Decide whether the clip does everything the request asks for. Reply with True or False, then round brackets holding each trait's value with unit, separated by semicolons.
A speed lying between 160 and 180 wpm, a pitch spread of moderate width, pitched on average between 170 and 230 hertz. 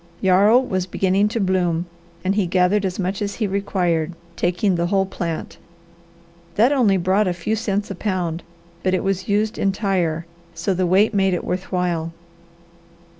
False (170 wpm; 2.2 semitones; 190 Hz)